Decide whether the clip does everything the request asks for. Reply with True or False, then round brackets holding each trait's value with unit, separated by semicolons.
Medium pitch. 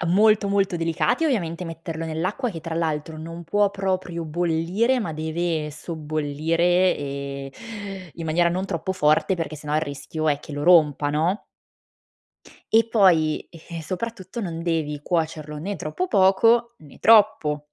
True (165 Hz)